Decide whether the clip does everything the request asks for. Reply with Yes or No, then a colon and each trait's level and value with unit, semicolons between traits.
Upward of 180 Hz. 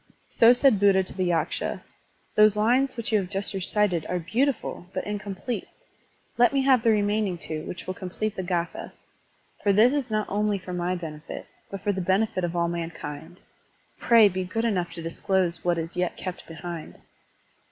Yes: high, 190 Hz